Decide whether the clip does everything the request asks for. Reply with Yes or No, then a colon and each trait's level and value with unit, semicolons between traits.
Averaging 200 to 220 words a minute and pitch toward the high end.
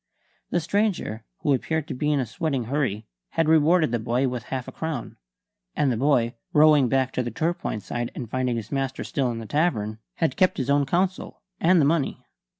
No: fast, 205 wpm; low, 135 Hz